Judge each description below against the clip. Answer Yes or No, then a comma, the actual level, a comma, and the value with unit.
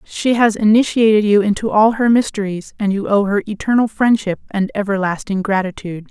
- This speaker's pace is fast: No, average, 165 wpm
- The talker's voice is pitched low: No, high, 210 Hz